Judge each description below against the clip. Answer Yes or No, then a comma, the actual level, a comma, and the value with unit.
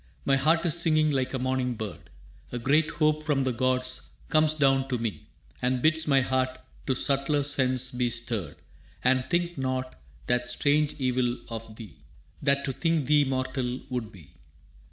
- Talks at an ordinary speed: Yes, average, 170 wpm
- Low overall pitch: Yes, low, 130 Hz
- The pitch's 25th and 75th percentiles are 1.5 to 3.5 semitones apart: Yes, average, 2.9 semitones